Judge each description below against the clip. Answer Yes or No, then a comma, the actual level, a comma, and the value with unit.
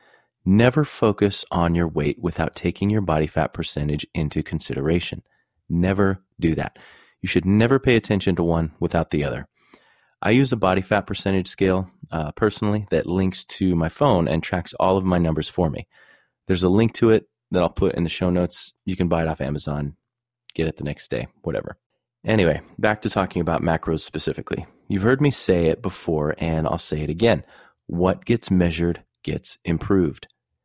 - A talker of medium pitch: No, very low, 90 Hz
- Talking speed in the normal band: Yes, average, 185 wpm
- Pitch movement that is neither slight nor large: Yes, average, 3.8 semitones